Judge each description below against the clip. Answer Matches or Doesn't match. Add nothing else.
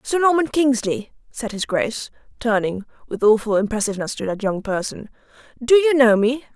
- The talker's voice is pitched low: Doesn't match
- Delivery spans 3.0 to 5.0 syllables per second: Doesn't match